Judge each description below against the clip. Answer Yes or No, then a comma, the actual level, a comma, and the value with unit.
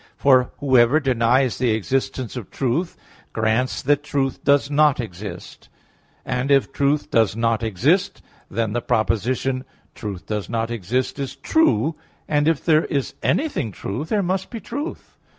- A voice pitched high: No, low, 130 Hz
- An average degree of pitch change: Yes, average, 4.3 semitones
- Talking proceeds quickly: No, average, 150 wpm